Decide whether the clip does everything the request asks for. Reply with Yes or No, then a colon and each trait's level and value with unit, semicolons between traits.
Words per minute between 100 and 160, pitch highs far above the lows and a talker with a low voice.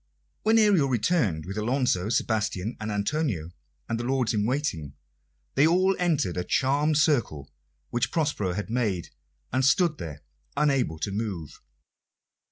Yes: average, 140 wpm; wide, 7.3 semitones; low, 120 Hz